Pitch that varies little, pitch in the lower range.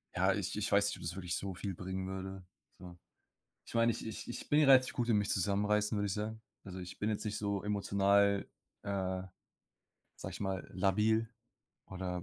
Yes: narrow, 2.0 semitones; low, 100 Hz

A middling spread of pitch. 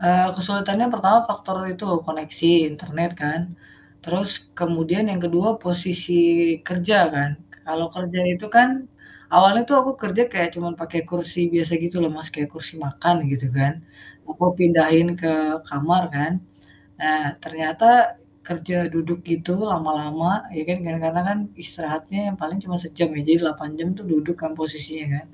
No: narrow, 2.3 semitones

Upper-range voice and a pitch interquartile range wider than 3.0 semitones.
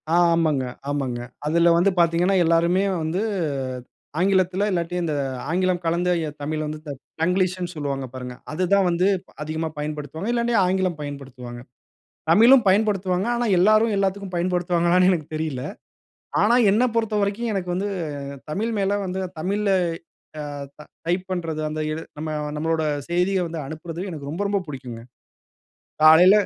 No: medium, 175 Hz; average, 3.8 semitones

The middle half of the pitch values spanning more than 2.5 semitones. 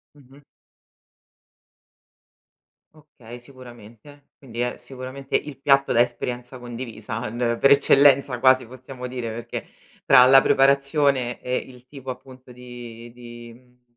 No: narrow, 2.0 semitones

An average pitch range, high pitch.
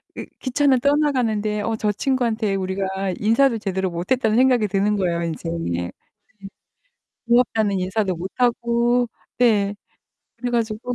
Yes: average, 3.9 semitones; high, 220 Hz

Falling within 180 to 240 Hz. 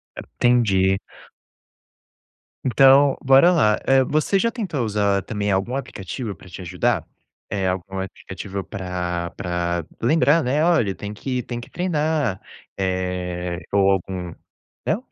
No: low, 100 Hz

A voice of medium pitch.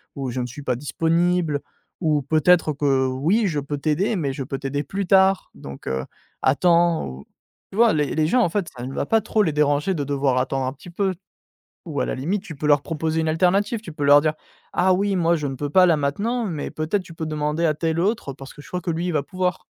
Yes: medium, 155 Hz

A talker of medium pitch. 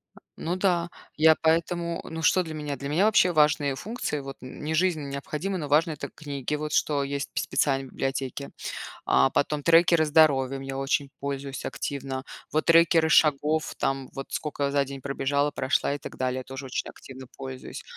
Yes: medium, 145 Hz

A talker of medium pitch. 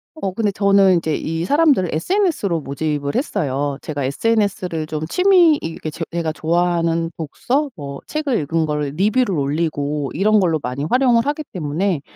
Yes: medium, 170 Hz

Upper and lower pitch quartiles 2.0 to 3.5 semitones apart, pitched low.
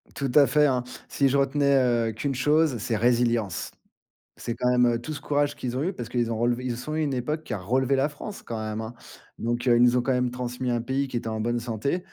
Yes: average, 2.8 semitones; low, 125 Hz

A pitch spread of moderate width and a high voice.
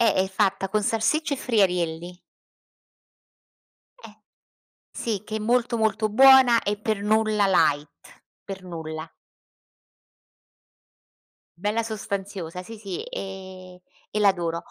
Yes: average, 3.1 semitones; high, 200 Hz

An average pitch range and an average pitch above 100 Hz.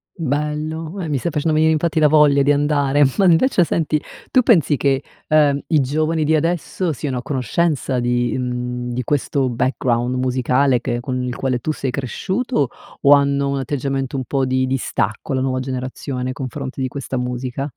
Yes: average, 3.1 semitones; medium, 140 Hz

